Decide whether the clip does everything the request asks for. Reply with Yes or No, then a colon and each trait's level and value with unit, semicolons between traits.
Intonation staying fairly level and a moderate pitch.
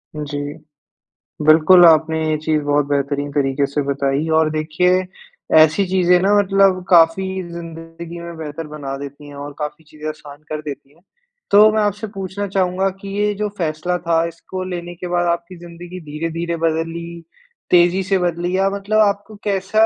No: average, 3.3 semitones; medium, 165 Hz